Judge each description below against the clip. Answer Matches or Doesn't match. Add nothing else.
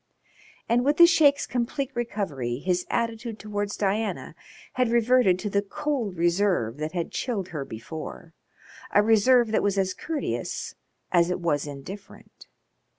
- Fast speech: Doesn't match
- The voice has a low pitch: Doesn't match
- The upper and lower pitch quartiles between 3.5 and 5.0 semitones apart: Doesn't match